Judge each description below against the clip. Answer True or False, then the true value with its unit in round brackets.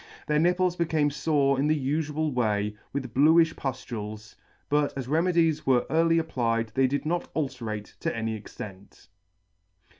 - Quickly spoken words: False (145 wpm)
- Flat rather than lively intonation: False (5.5 semitones)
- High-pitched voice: False (140 Hz)